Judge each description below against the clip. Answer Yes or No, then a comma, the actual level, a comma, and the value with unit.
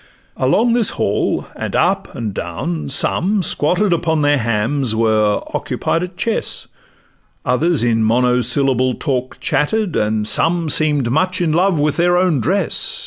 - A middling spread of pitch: No, wide, 6.3 semitones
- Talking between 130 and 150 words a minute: Yes, average, 140 wpm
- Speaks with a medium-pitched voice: Yes, medium, 145 Hz